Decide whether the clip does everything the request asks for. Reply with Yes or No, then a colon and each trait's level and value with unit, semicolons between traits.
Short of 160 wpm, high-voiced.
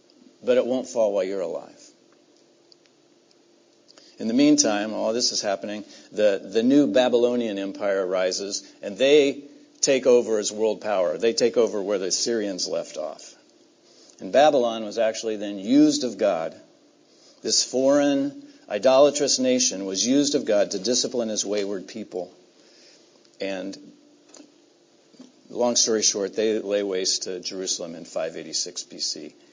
Yes: average, 140 wpm; high, 225 Hz